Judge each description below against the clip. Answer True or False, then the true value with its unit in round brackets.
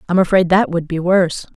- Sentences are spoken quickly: True (225 wpm)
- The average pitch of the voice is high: False (180 Hz)